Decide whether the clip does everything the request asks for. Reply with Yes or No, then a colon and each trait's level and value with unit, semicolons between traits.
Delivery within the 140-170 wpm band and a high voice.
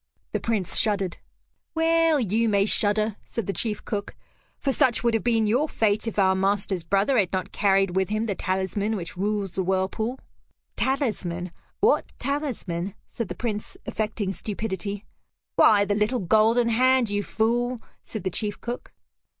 Yes: average, 160 wpm; high, 210 Hz